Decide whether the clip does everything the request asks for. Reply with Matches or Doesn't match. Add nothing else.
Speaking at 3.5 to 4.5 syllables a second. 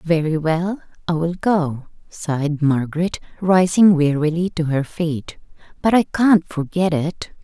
Matches